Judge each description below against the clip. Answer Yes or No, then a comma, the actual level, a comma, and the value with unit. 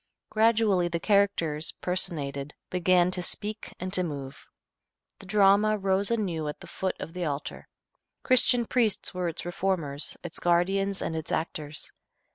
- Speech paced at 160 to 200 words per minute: No, average, 145 wpm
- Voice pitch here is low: No, medium, 180 Hz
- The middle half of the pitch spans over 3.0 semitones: Yes, average, 3.6 semitones